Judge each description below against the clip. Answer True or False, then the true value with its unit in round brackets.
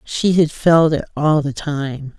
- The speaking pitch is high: False (150 Hz)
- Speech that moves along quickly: False (190 wpm)